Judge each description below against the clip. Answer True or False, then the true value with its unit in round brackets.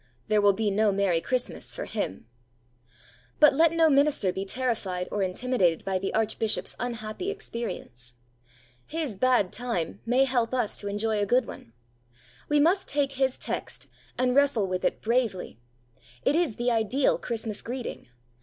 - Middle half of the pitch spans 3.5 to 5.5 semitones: True (4.7 semitones)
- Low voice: False (230 Hz)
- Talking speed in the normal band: True (155 wpm)